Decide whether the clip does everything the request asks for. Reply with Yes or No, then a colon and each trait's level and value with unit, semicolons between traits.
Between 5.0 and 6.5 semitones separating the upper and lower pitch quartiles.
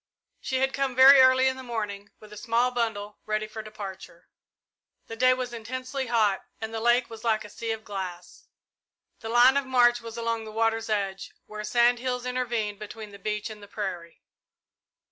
No: average, 2.8 semitones